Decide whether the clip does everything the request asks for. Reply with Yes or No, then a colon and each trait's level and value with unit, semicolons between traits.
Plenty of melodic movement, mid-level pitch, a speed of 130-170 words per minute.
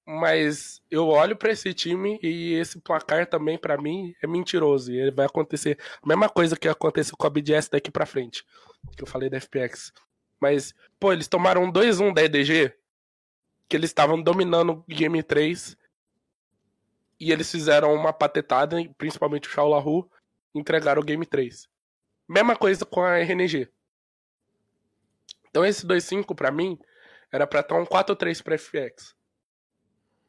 No: average, 3.3 semitones; medium, 160 Hz; average, 155 wpm